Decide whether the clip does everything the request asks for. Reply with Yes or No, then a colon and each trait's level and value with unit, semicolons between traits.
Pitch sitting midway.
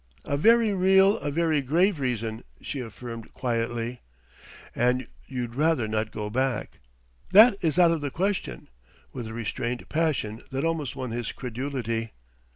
No: low, 130 Hz